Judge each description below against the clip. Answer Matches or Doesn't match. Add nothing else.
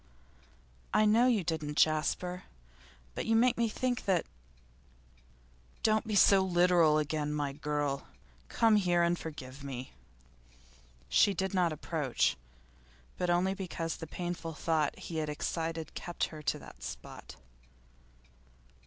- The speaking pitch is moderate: Matches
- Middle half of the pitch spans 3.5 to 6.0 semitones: Matches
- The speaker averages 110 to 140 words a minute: Matches